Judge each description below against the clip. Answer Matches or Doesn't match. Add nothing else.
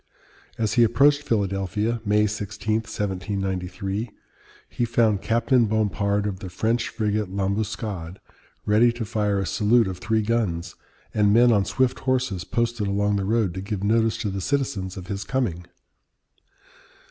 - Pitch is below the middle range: Matches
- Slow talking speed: Doesn't match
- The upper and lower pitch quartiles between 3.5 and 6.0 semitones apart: Doesn't match